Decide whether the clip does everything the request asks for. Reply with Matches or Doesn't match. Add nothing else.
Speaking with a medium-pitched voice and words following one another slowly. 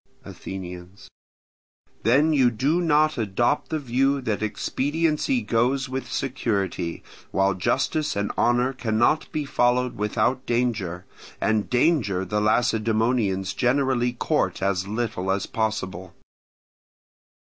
Doesn't match